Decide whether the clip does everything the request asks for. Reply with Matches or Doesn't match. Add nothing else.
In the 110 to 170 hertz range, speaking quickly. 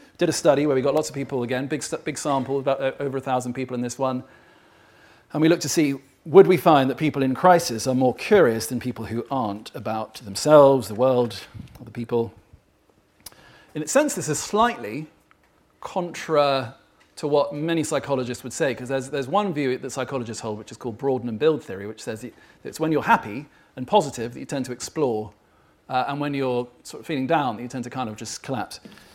Matches